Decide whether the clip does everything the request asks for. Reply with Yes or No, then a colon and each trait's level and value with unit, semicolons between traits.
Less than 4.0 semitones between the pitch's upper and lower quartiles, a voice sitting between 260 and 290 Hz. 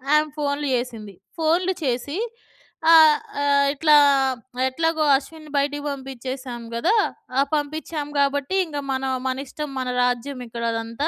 Yes: average, 2.9 semitones; very high, 280 Hz